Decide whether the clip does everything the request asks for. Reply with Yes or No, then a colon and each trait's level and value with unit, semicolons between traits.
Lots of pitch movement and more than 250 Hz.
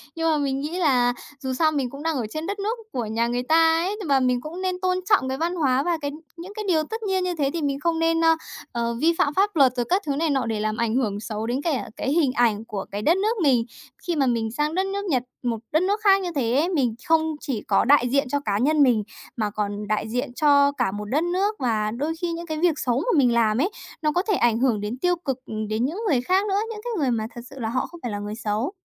Yes: wide, 6.1 semitones; very high, 280 Hz